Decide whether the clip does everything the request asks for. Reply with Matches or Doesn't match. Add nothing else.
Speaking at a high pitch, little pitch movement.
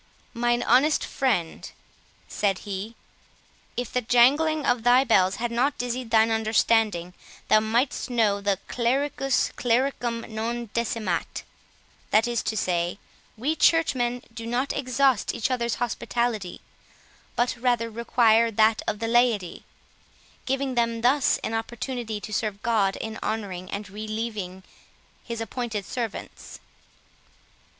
Matches